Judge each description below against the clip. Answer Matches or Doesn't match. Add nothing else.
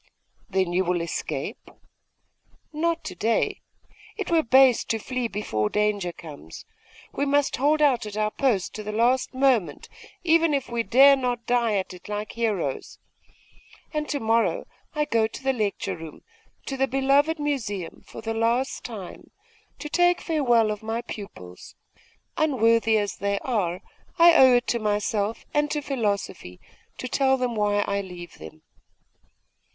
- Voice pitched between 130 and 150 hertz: Doesn't match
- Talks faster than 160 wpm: Doesn't match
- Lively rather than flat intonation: Doesn't match